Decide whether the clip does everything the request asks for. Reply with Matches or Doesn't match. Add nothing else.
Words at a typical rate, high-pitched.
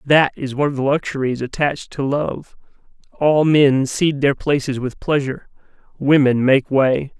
Doesn't match